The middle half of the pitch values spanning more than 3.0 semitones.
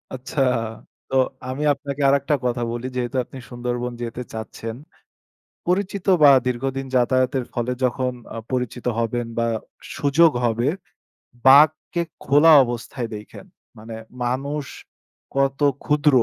No: average, 2.7 semitones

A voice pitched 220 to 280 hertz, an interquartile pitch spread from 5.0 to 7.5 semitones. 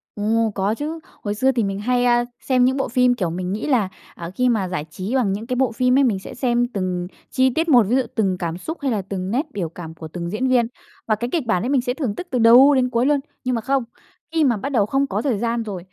No: high, 235 Hz; average, 4.6 semitones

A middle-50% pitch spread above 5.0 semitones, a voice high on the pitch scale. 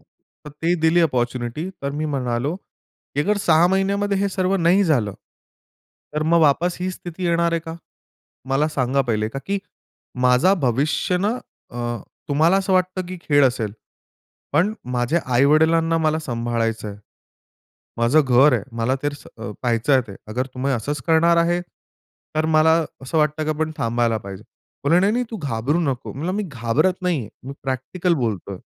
No: wide, 5.6 semitones; medium, 150 Hz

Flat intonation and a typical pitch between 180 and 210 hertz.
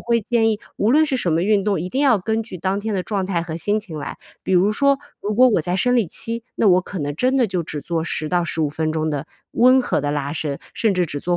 No: wide, 5.6 semitones; high, 190 Hz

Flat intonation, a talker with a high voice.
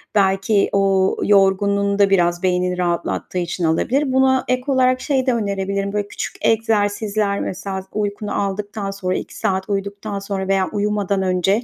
Yes: narrow, 1.6 semitones; high, 200 Hz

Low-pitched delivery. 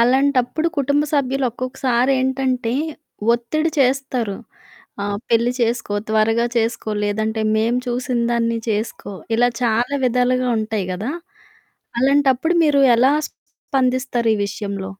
No: high, 245 Hz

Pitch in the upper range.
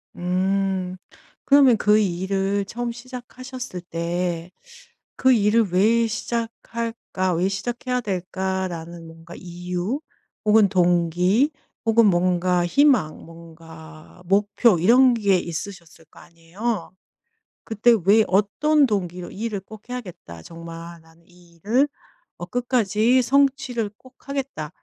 Yes: high, 195 Hz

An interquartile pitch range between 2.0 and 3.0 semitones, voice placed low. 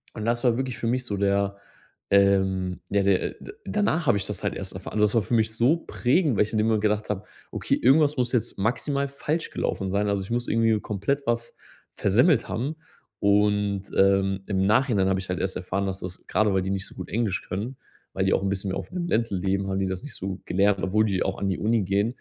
No: average, 3.5 semitones; low, 105 Hz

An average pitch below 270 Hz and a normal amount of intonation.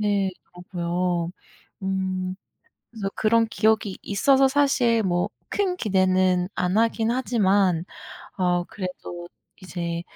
Yes: high, 190 Hz; average, 3.7 semitones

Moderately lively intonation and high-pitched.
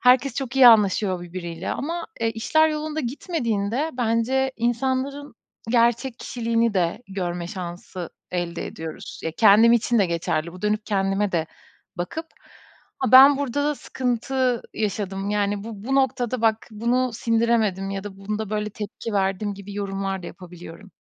Yes: average, 4.5 semitones; high, 220 Hz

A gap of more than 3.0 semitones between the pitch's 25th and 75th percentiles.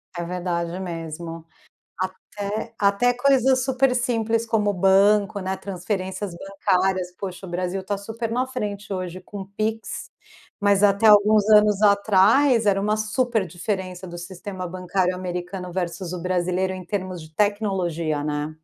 No: average, 2.7 semitones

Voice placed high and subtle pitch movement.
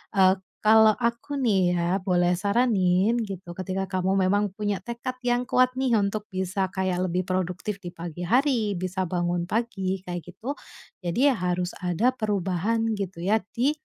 No: high, 195 Hz; average, 3.6 semitones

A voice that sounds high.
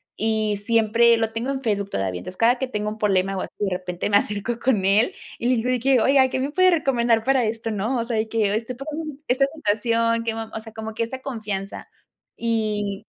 Yes: high, 225 Hz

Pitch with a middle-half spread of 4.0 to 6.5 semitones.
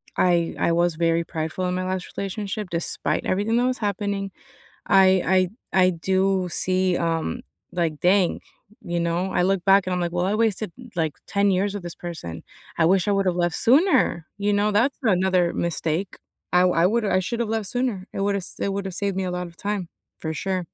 No: narrow, 2.6 semitones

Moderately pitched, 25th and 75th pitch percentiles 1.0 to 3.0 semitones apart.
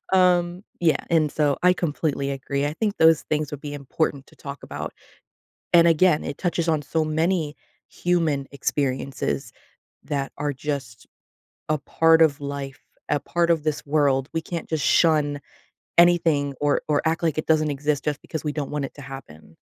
Yes: medium, 150 Hz; narrow, 2.5 semitones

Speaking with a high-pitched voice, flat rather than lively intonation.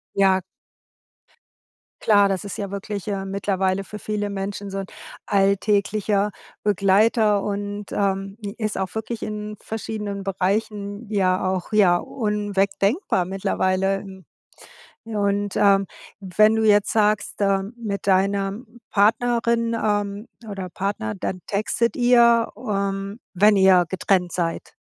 Yes: high, 200 Hz; narrow, 1.5 semitones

